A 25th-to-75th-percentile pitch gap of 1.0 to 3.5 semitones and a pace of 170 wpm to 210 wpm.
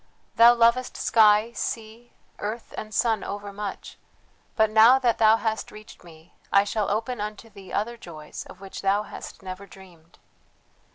No: narrow, 2.5 semitones; average, 155 wpm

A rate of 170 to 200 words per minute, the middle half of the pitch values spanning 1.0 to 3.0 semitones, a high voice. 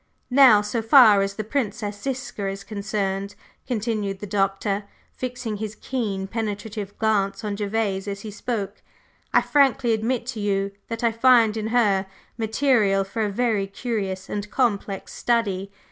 No: average, 150 wpm; average, 2.7 semitones; high, 210 Hz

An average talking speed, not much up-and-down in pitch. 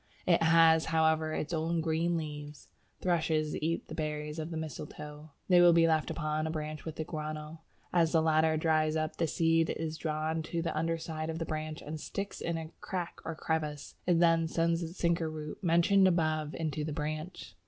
Yes: average, 195 wpm; narrow, 1.2 semitones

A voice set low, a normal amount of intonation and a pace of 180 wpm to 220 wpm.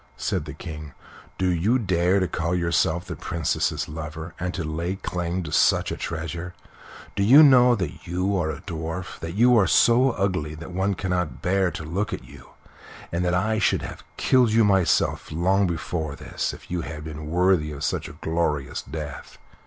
Yes: very low, 90 Hz; average, 3.3 semitones; average, 190 wpm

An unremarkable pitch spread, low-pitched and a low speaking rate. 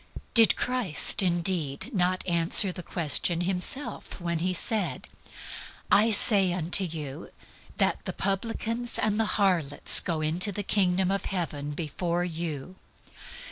No: average, 3.2 semitones; medium, 180 Hz; slow, 130 wpm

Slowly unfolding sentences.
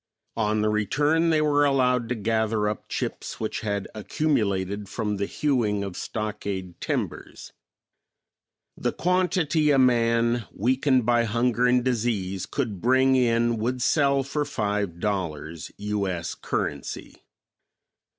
Yes: slow, 130 wpm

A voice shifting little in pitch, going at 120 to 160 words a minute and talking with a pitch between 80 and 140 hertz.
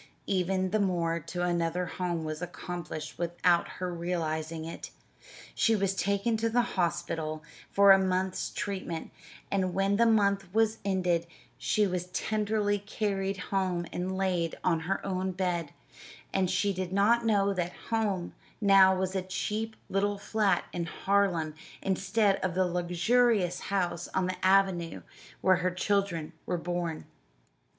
No: narrow, 2.3 semitones; average, 145 wpm; medium, 185 Hz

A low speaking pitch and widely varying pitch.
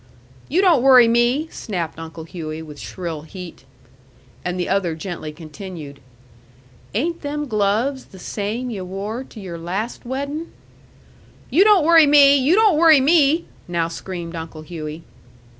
No: high, 205 Hz; wide, 8.9 semitones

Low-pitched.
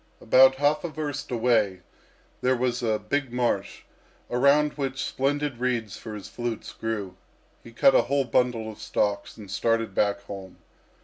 Yes: low, 120 Hz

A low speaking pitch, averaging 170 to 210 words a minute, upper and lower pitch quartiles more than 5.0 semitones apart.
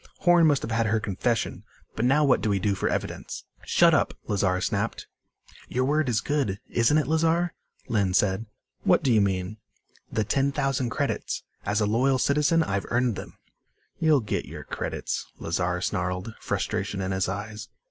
Yes: low, 115 Hz; average, 175 wpm; wide, 5.6 semitones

